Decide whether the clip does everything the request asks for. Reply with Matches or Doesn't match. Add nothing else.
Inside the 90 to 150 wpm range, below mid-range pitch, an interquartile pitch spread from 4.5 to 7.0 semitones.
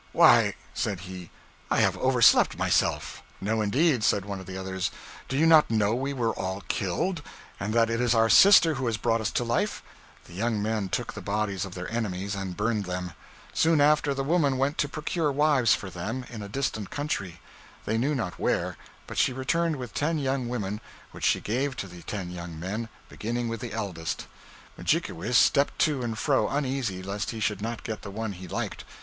Doesn't match